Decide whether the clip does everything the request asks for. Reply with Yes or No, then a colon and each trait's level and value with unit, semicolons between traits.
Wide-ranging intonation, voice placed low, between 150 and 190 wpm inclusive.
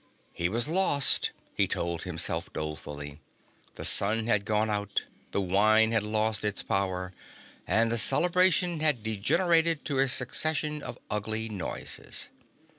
No: wide, 6.5 semitones; low, 110 Hz; slow, 135 wpm